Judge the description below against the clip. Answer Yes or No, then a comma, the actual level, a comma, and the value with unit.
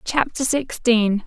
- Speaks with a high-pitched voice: Yes, high, 235 Hz